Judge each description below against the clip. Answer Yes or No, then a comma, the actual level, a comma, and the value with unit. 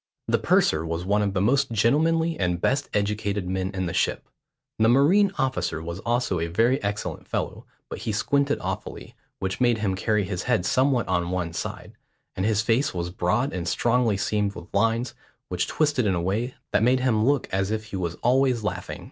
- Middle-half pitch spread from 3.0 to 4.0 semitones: No, average, 5.1 semitones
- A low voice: Yes, low, 105 Hz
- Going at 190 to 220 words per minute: Yes, average, 200 wpm